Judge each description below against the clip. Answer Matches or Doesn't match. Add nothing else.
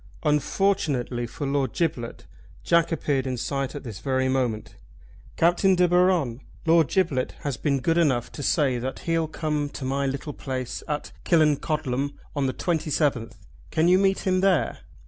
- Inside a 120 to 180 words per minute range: Matches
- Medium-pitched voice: Matches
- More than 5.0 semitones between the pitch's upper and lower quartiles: Doesn't match